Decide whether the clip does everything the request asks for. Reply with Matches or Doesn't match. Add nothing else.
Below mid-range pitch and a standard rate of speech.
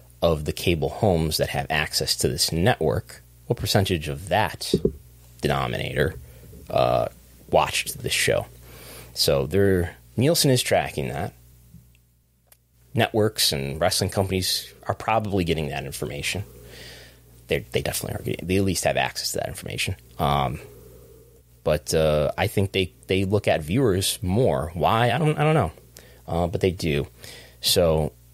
Matches